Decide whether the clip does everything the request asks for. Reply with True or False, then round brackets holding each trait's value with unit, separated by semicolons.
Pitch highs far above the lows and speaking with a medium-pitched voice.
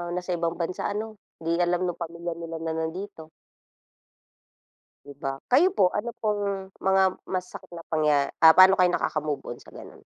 False (3.0 semitones; 175 Hz)